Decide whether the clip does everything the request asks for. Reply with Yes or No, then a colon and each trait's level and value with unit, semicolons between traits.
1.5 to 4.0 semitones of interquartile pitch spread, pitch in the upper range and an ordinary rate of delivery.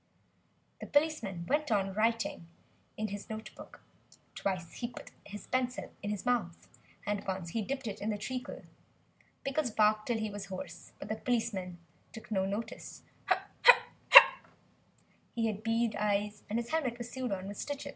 Yes: average, 3.2 semitones; high, 215 Hz; average, 165 wpm